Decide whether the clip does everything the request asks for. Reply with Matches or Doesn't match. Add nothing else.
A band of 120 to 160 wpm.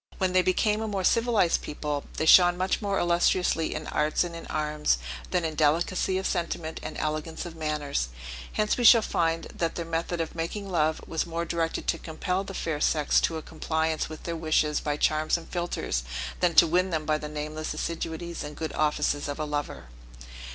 Doesn't match